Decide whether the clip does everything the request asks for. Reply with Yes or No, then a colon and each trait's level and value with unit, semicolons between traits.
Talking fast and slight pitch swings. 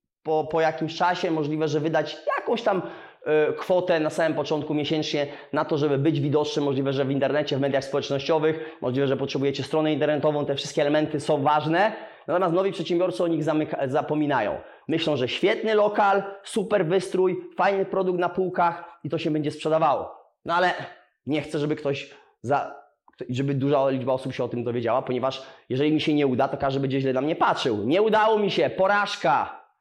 No: fast, 185 wpm; average, 3.7 semitones